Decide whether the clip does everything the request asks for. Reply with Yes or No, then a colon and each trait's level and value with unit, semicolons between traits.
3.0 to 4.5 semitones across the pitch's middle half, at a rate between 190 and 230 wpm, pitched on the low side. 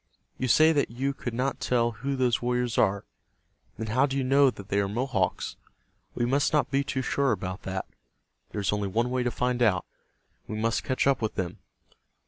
Yes: average, 3.8 semitones; fast, 205 wpm; low, 125 Hz